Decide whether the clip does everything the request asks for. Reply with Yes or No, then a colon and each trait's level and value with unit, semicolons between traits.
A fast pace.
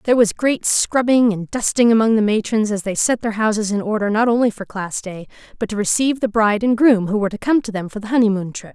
Yes: fast, 260 wpm